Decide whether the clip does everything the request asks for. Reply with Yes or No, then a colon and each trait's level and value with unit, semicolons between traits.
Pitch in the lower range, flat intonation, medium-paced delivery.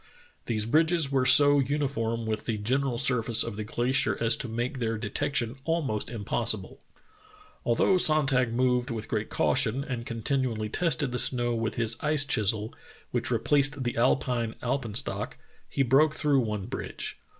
No: low, 120 Hz; average, 3.5 semitones; average, 160 wpm